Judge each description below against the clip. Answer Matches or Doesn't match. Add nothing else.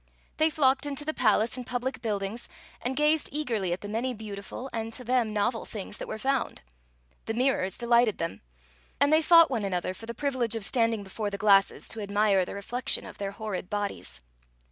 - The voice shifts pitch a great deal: Doesn't match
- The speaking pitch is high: Matches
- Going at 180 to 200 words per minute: Matches